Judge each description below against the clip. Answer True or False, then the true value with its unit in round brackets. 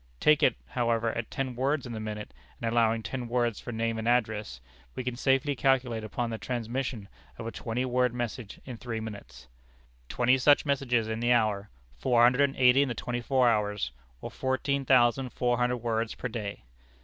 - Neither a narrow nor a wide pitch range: False (2.3 semitones)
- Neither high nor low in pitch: False (120 Hz)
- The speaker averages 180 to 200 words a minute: True (195 wpm)